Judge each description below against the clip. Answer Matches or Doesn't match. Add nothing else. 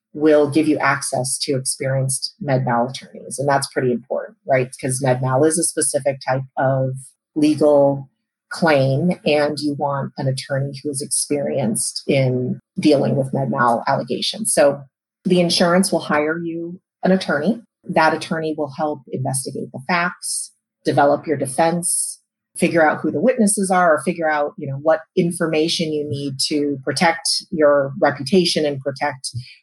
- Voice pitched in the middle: Matches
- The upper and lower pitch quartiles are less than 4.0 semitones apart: Matches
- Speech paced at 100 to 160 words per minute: Matches